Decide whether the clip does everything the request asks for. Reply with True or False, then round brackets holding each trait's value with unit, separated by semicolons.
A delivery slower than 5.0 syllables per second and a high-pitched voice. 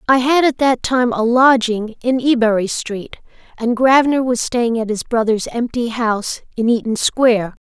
True (4.7 syllables/s; 235 Hz)